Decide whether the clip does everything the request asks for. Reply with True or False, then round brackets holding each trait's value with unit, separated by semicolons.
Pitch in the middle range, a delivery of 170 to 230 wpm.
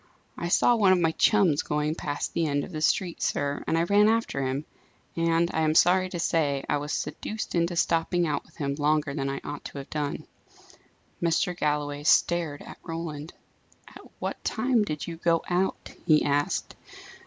True (160 Hz; 190 wpm)